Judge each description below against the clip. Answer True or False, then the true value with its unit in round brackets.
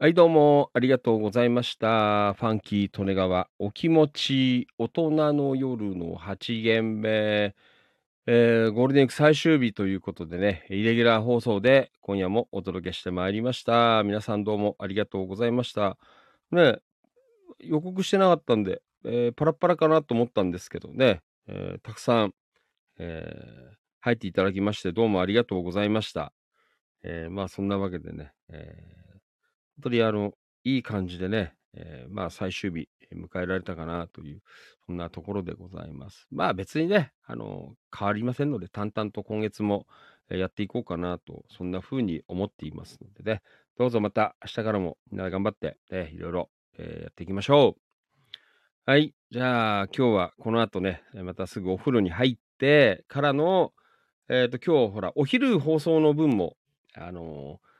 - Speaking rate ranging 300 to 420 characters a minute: True (345 characters per minute)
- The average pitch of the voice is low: True (110 Hz)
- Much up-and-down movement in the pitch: False (4.8 semitones)